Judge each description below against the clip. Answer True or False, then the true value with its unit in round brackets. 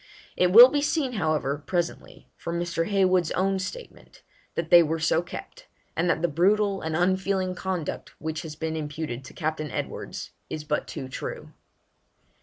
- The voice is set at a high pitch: False (170 Hz)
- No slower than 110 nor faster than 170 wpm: True (165 wpm)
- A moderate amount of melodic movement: True (3.3 semitones)